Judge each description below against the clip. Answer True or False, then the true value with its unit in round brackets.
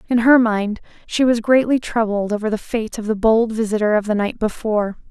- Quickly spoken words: True (210 wpm)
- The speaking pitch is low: False (220 Hz)